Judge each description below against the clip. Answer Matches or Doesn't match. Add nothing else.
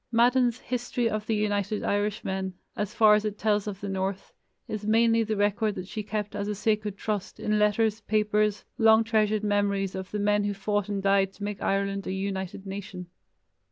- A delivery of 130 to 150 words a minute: Doesn't match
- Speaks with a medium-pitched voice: Doesn't match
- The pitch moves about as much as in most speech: Doesn't match